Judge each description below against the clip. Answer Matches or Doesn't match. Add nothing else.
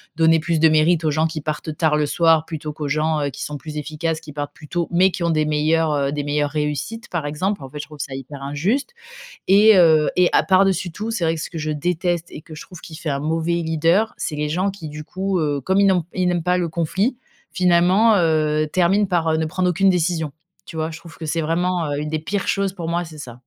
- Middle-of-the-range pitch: Matches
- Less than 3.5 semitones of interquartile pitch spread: Matches